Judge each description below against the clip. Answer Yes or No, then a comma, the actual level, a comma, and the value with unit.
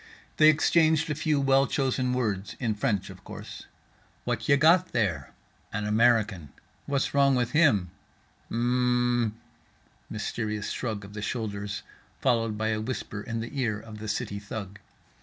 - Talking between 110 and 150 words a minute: Yes, average, 140 wpm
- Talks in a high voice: No, low, 115 Hz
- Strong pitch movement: No, average, 4.3 semitones